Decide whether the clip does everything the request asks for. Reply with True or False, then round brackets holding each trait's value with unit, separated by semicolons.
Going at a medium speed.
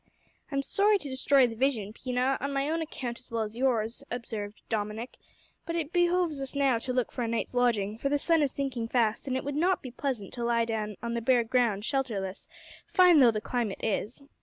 False (220 wpm)